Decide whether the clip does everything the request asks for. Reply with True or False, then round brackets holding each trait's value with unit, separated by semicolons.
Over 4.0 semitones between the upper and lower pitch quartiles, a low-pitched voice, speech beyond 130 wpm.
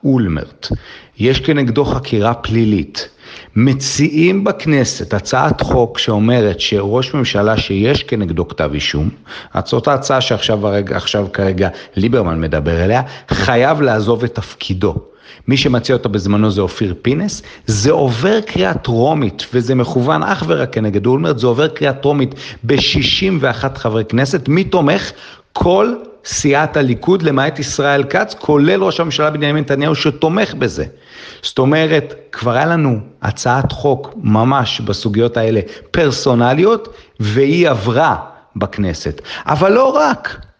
False (5.1 semitones; 125 Hz; 125 wpm)